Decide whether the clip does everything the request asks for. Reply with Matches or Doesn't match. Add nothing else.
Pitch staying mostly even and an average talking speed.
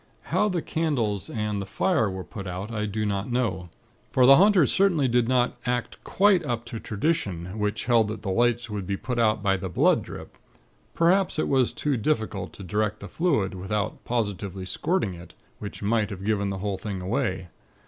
Doesn't match